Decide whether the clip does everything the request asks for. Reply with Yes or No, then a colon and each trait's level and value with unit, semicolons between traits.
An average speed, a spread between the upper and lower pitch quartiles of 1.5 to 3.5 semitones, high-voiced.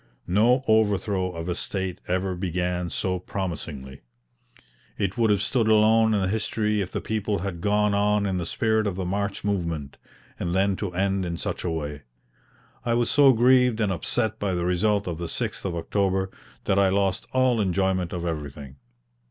No: average, 180 wpm; average, 3.2 semitones; very low, 95 Hz